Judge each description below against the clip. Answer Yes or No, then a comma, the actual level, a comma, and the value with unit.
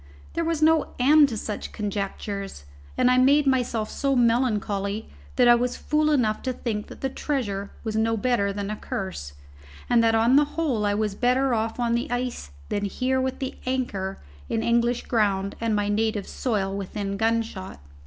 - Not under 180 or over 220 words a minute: Yes, average, 185 wpm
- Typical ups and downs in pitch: Yes, average, 3.8 semitones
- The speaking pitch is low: No, high, 230 Hz